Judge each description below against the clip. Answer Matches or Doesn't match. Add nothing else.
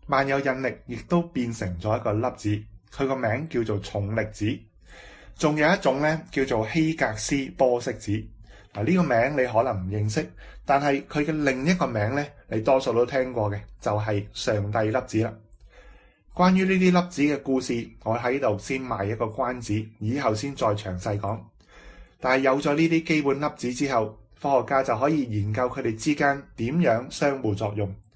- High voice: Doesn't match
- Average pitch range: Matches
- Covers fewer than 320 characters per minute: Matches